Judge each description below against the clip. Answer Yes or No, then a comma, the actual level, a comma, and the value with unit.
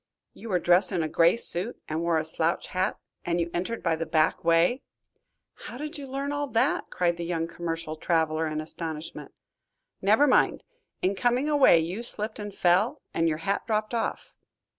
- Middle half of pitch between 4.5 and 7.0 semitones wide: Yes, wide, 5.5 semitones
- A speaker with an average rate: Yes, average, 185 wpm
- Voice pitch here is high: No, medium, 175 Hz